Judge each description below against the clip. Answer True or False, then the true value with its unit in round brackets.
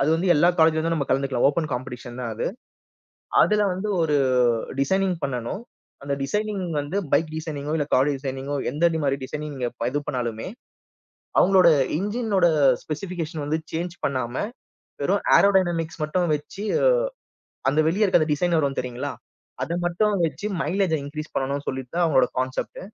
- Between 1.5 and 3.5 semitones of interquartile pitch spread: False (4.3 semitones)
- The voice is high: False (155 Hz)